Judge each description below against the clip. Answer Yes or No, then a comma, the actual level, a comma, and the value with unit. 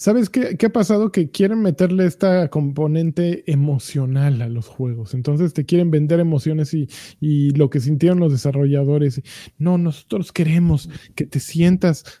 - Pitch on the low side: No, medium, 155 Hz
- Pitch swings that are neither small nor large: Yes, average, 3.7 semitones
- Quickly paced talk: No, average, 155 wpm